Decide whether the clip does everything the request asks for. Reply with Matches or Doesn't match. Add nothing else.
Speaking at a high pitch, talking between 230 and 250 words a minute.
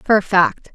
Matches